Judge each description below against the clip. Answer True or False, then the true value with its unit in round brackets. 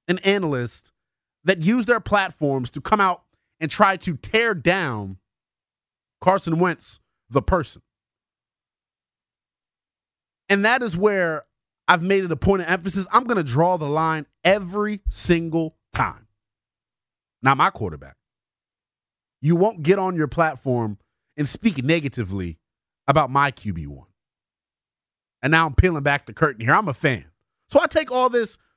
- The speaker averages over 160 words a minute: False (140 wpm)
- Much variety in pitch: True (6.9 semitones)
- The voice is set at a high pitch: False (160 Hz)